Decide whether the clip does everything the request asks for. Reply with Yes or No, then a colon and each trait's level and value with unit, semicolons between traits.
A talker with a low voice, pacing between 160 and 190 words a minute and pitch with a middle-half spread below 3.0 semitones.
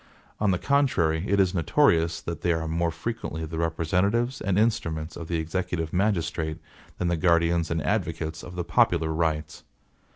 Yes: very low, 85 Hz; average, 165 wpm; narrow, 2.4 semitones